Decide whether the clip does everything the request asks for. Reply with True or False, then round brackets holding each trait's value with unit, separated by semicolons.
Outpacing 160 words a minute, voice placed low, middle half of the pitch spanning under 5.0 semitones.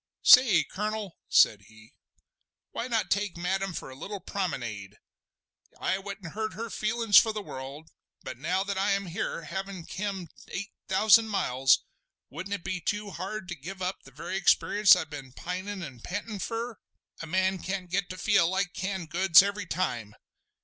False (170 wpm; 190 Hz; 3.6 semitones)